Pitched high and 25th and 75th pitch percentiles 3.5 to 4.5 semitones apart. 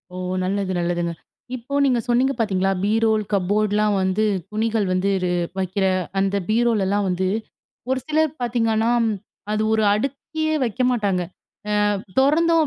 Yes: high, 215 Hz; average, 3.9 semitones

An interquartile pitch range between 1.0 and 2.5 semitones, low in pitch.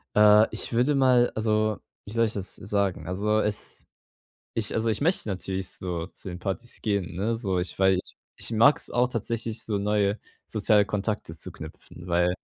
No: average, 2.9 semitones; low, 105 Hz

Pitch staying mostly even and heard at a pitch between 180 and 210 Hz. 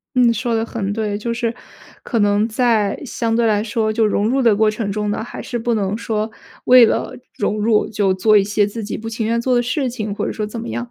No: narrow, 2.0 semitones; high, 220 Hz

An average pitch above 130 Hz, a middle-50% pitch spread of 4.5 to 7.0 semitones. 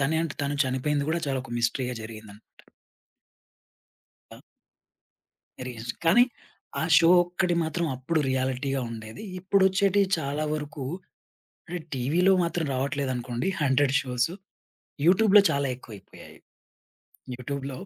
Yes: medium, 140 Hz; average, 4.8 semitones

